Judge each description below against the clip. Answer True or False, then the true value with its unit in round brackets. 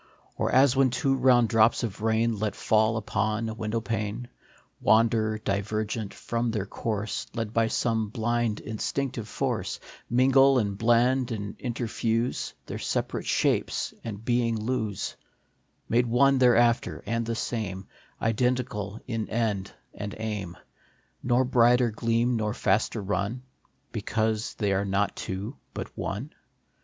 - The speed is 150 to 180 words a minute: False (135 wpm)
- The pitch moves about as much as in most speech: False (2.2 semitones)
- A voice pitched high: False (115 Hz)